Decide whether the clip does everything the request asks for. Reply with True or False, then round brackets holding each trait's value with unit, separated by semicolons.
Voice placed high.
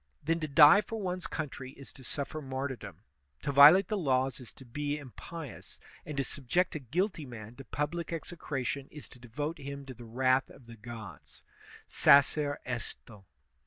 False (140 Hz)